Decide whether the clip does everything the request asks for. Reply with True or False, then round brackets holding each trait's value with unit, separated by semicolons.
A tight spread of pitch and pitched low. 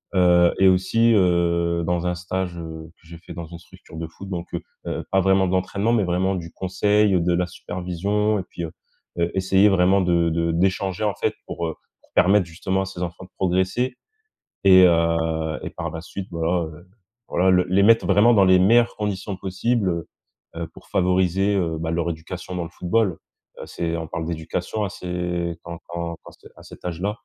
True (2.2 semitones; 90 Hz)